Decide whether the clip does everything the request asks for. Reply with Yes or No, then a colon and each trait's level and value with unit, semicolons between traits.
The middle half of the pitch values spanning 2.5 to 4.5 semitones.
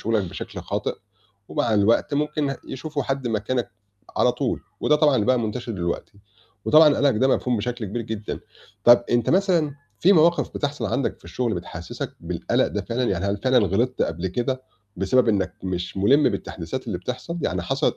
No: wide, 5.4 semitones